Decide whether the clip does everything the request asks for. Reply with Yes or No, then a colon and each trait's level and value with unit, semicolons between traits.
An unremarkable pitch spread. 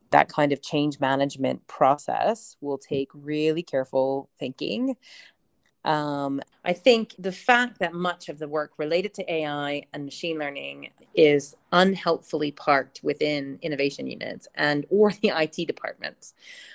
Yes: average, 4.0 semitones